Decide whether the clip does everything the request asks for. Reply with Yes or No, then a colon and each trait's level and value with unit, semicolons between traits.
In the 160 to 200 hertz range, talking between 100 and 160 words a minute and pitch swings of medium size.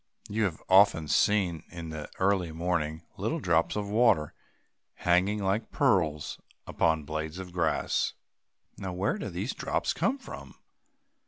No: very low, 90 Hz; average, 145 wpm; average, 4.0 semitones